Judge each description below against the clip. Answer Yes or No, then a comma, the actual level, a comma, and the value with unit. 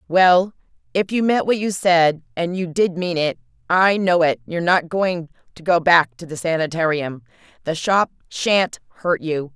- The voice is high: No, medium, 170 Hz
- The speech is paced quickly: No, average, 170 wpm